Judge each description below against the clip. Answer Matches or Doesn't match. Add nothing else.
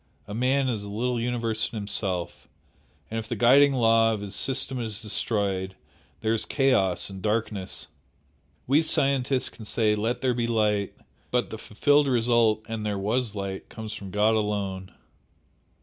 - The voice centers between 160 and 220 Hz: Doesn't match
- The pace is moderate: Matches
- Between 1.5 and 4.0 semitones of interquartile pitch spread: Matches